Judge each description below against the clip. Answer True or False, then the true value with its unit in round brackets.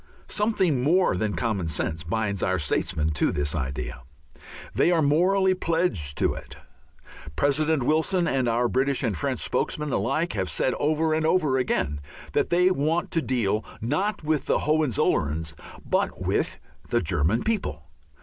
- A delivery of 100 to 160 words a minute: True (150 wpm)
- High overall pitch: False (130 Hz)